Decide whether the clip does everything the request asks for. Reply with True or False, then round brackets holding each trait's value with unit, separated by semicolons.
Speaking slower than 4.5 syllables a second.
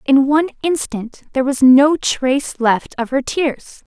True (4.3 syllables/s)